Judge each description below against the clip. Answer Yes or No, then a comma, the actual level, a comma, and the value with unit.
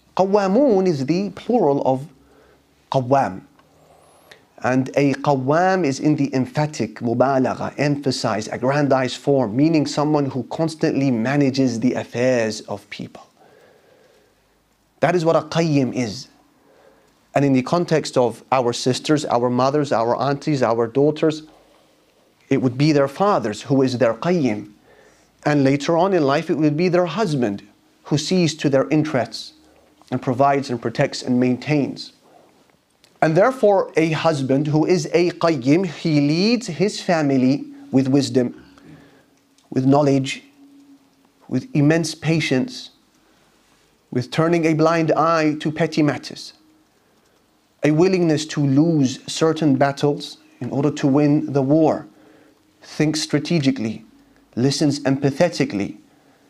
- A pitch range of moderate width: Yes, average, 3.6 semitones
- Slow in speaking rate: Yes, slow, 125 wpm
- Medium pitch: Yes, medium, 145 Hz